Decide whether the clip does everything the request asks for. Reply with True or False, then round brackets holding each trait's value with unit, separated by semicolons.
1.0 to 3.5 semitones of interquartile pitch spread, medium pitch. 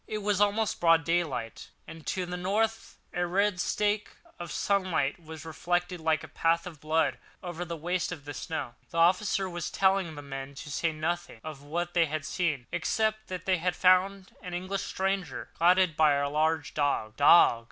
True (3.1 semitones; 175 Hz)